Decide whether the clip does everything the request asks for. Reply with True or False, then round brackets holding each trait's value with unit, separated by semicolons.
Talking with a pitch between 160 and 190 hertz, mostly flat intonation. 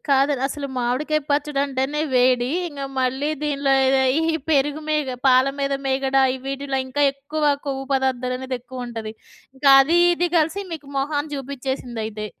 False (275 Hz; 2.1 semitones)